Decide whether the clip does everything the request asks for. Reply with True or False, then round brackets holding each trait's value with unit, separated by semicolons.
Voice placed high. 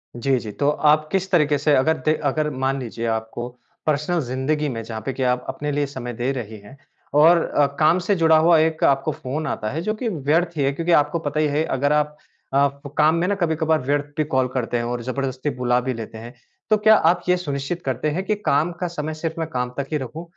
False (145 Hz)